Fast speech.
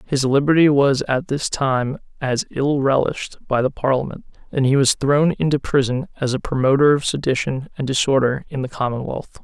No: average, 180 wpm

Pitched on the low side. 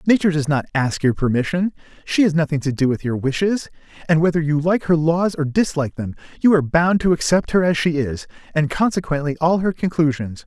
No: medium, 160 Hz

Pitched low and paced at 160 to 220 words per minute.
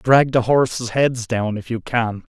Yes: low, 120 Hz; fast, 205 wpm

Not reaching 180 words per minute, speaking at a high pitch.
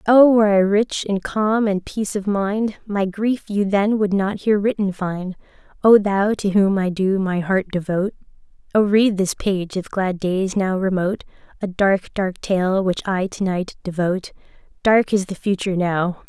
No: average, 185 wpm; high, 195 Hz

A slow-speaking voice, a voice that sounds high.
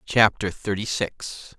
No: slow, 115 wpm; low, 100 Hz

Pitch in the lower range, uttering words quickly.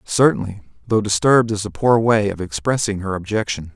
No: low, 100 Hz; average, 160 wpm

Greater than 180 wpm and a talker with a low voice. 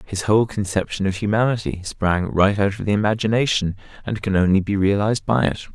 Yes: average, 190 wpm; low, 100 Hz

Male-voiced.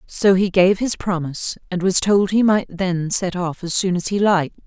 No: female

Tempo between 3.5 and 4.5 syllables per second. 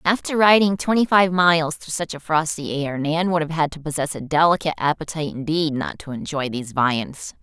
No: 5.6 syllables/s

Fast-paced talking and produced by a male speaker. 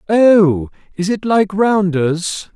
No: slow, 120 wpm; male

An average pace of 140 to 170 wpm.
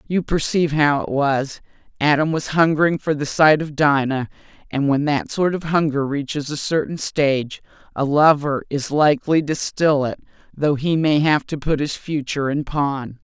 No: average, 180 wpm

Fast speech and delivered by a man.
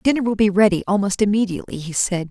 No: fast, 210 wpm; female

